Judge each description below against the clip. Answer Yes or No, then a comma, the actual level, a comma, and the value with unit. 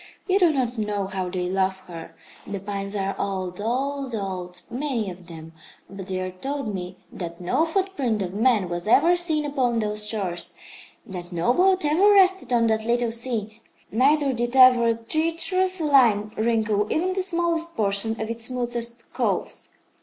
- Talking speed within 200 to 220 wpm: No, average, 170 wpm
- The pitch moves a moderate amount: No, wide, 6.4 semitones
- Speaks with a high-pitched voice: Yes, high, 230 Hz